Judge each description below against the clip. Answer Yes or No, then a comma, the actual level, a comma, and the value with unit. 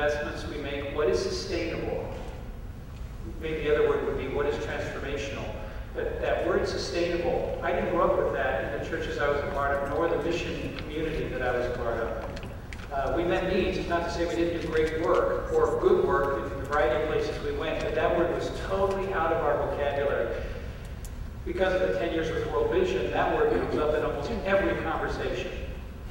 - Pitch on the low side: No, medium, 175 Hz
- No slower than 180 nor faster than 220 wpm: Yes, fast, 205 wpm